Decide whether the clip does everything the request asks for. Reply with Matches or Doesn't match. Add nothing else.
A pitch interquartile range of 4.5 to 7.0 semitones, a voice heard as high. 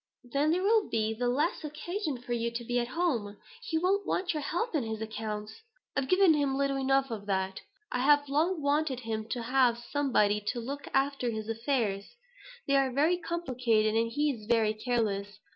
Matches